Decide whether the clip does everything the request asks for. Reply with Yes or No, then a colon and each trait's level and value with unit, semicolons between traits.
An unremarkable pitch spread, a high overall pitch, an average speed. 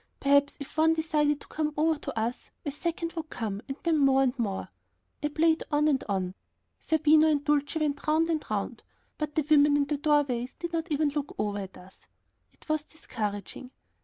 Yes: average, 3.4 semitones; very high, 295 Hz; average, 190 wpm